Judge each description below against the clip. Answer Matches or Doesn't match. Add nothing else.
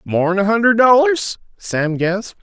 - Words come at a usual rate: Matches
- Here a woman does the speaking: Doesn't match